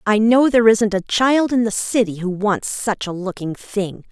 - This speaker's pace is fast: Yes, fast, 220 wpm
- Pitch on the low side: No, high, 215 Hz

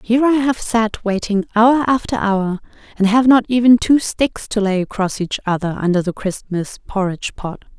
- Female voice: Yes, female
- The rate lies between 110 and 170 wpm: No, average, 185 wpm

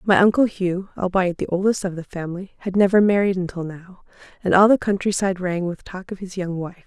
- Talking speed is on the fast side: Yes, fast, 220 wpm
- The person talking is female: Yes, female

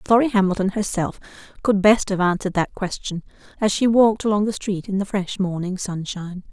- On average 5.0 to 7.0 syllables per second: Yes, 5.7 syllables/s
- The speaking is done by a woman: Yes, female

